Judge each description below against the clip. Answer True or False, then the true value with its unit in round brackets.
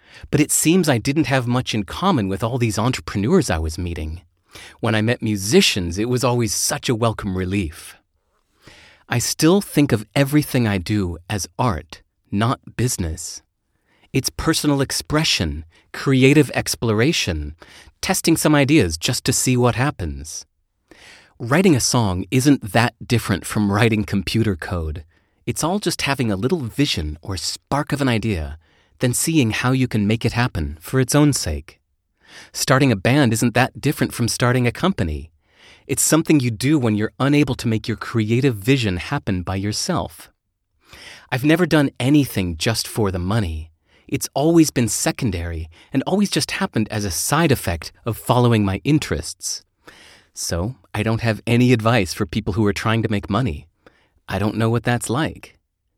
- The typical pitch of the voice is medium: False (115 Hz)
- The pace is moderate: True (165 wpm)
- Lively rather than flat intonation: True (5.8 semitones)